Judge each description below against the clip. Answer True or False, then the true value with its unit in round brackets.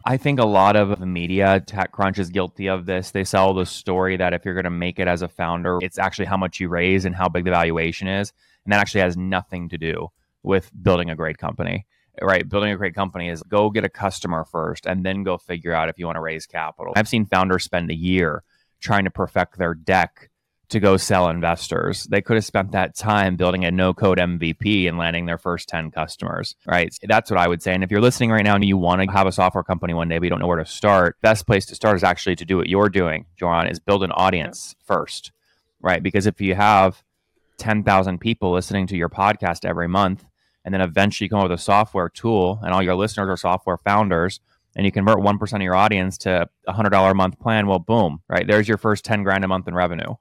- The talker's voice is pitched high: False (95 Hz)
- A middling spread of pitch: False (2.3 semitones)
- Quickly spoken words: True (245 wpm)